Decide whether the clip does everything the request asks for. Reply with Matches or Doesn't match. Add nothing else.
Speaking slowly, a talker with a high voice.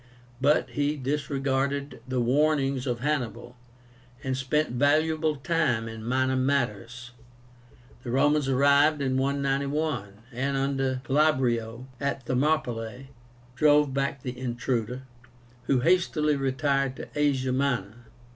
Doesn't match